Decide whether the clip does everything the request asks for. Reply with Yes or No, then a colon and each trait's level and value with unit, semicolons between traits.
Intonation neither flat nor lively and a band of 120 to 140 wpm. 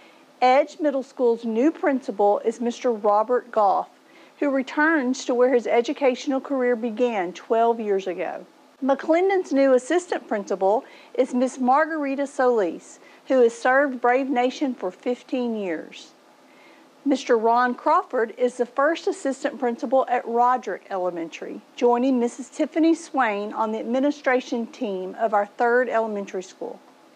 Yes: average, 3.1 semitones; slow, 135 wpm